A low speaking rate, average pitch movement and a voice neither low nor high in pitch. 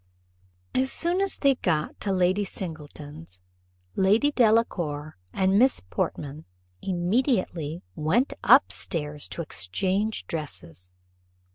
No: slow, 105 wpm; wide, 6.6 semitones; medium, 180 Hz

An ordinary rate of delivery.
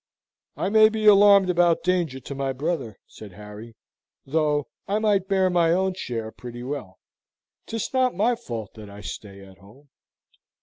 Yes: average, 165 wpm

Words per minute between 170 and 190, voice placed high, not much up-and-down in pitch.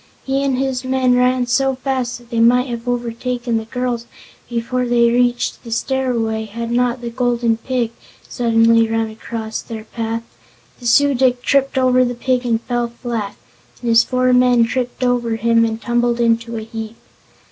Yes: average, 175 wpm; high, 240 Hz; narrow, 1.6 semitones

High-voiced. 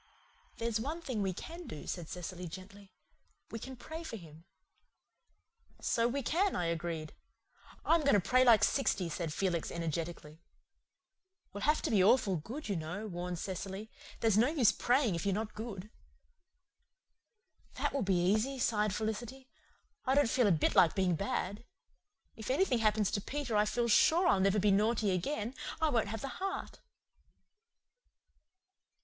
Yes: high, 210 Hz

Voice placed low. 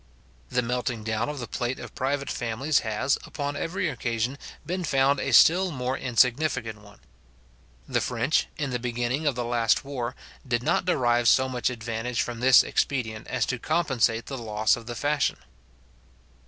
Yes: low, 125 Hz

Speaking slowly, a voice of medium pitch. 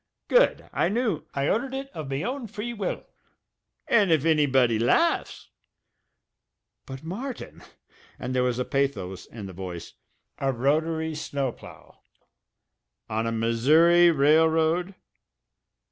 Yes: slow, 130 wpm; medium, 155 Hz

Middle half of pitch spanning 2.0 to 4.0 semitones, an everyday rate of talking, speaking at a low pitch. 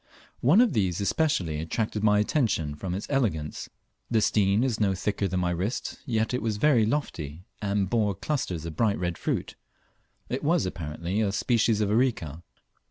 No: average, 4.8 semitones; average, 170 wpm; low, 105 Hz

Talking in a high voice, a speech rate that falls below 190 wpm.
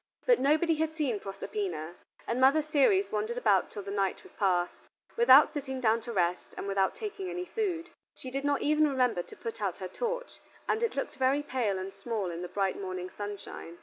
No: very high, 250 Hz; fast, 205 wpm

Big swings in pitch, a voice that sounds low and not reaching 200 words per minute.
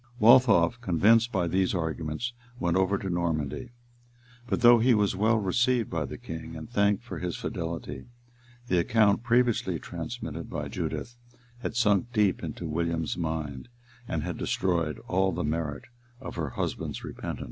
Yes: wide, 5.7 semitones; very low, 95 Hz; average, 155 wpm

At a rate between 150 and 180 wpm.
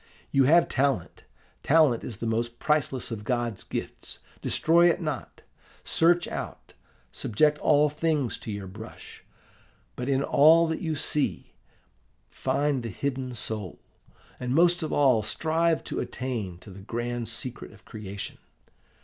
No: average, 140 wpm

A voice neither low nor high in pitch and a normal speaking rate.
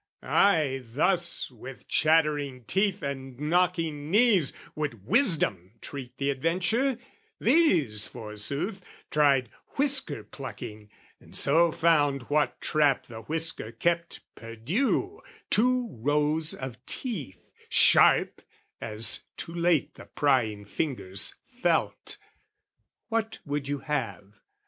No: medium, 145 Hz; slow, 105 wpm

